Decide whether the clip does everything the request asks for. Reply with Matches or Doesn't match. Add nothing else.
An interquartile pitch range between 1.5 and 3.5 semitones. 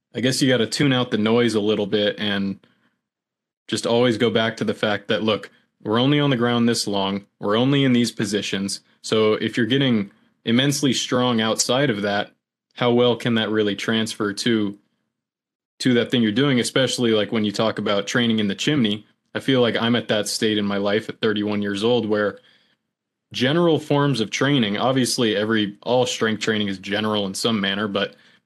Matches